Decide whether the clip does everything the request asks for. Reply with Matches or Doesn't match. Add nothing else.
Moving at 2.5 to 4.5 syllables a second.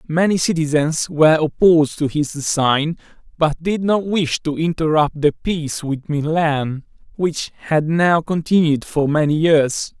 Matches